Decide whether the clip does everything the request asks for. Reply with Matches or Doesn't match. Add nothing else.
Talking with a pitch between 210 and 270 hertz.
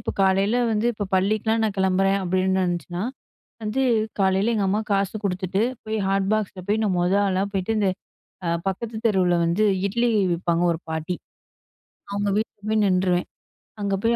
Doesn't match